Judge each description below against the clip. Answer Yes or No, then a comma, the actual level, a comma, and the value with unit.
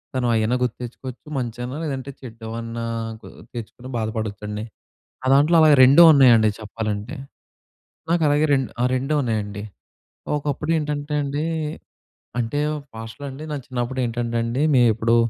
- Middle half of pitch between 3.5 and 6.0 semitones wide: Yes, average, 4.2 semitones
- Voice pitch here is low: Yes, low, 125 Hz